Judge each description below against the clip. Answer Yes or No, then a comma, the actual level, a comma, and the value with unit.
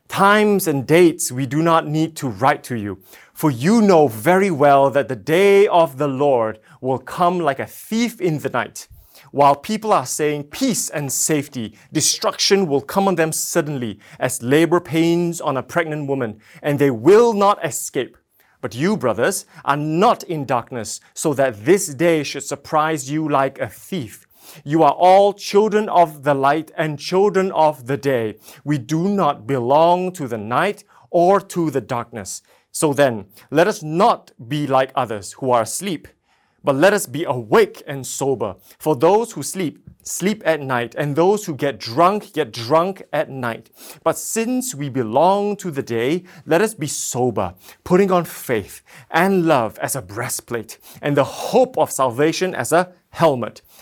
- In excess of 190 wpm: No, average, 175 wpm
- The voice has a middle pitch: Yes, medium, 155 Hz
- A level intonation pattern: No, average, 4.6 semitones